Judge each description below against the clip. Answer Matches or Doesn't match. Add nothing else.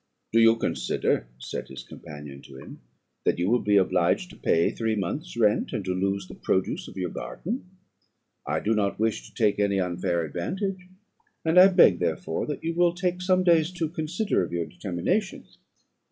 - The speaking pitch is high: Doesn't match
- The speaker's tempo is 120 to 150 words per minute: Doesn't match